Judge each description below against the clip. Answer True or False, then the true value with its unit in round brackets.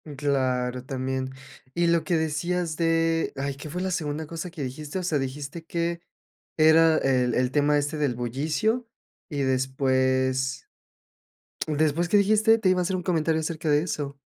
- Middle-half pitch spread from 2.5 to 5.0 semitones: True (4.1 semitones)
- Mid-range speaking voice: True (150 Hz)